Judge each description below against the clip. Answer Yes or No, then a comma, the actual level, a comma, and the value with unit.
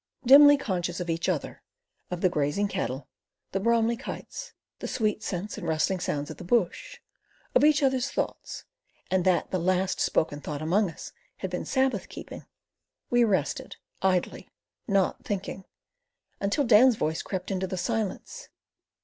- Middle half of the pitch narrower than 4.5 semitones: No, average, 4.8 semitones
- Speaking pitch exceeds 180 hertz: Yes, high, 190 Hz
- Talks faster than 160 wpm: No, average, 155 wpm